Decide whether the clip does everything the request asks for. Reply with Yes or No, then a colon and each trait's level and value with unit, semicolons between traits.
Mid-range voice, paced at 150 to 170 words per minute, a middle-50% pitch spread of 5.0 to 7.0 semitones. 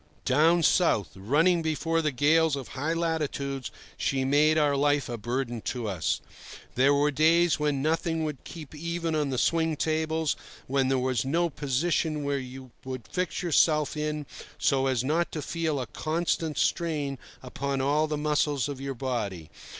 No: medium, 145 Hz; average, 165 wpm; average, 3.3 semitones